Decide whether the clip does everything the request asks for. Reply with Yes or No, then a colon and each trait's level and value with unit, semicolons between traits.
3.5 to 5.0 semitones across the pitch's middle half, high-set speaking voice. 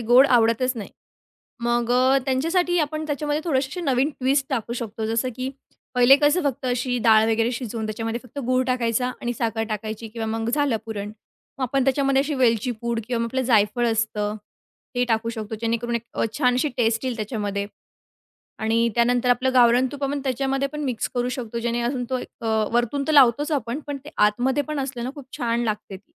No: average, 2.9 semitones; high, 245 Hz